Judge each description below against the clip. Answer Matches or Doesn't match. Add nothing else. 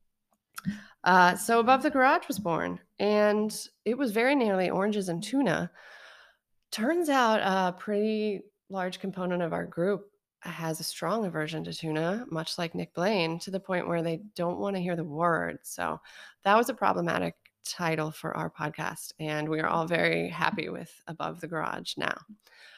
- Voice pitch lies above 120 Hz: Matches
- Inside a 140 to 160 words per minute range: Doesn't match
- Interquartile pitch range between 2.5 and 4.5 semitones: Matches